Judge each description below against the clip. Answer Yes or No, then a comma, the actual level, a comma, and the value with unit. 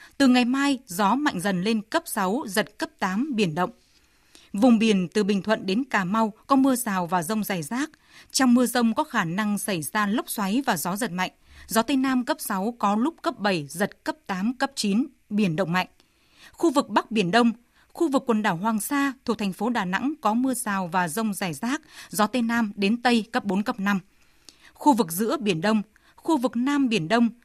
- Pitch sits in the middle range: No, high, 225 Hz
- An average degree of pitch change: Yes, average, 4.3 semitones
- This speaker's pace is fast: No, average, 225 wpm